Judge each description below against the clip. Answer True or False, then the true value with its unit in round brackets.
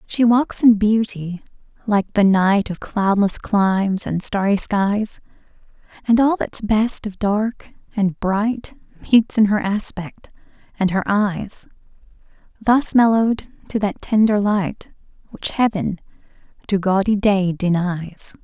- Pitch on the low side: False (205 Hz)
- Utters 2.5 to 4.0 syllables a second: True (3.6 syllables/s)